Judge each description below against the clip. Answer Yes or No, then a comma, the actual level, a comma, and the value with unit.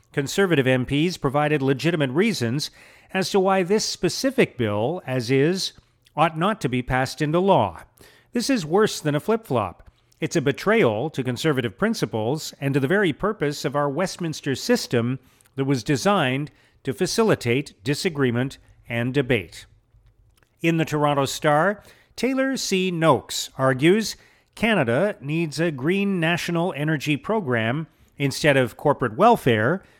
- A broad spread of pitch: Yes, wide, 6.1 semitones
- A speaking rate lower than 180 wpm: Yes, average, 140 wpm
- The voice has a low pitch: No, medium, 150 Hz